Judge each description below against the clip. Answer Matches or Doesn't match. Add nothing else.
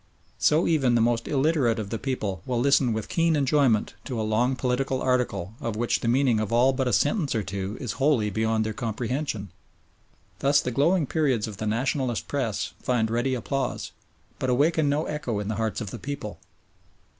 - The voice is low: Matches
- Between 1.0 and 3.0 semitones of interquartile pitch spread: Doesn't match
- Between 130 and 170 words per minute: Doesn't match